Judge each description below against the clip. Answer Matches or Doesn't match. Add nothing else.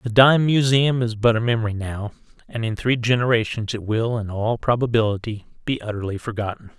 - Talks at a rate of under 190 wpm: Matches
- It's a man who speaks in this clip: Matches